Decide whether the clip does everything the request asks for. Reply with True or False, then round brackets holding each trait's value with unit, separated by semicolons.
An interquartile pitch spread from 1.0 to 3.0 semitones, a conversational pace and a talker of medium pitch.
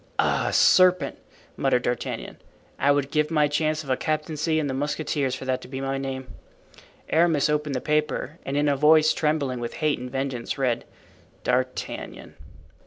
True (2.5 semitones; 170 wpm; 145 Hz)